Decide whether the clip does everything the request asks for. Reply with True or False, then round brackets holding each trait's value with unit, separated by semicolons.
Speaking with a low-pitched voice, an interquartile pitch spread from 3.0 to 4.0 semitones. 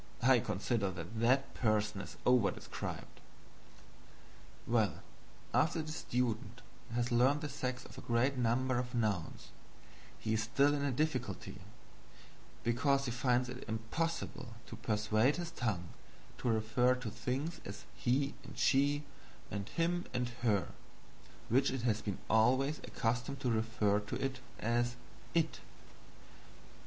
True (120 Hz; 3.6 semitones)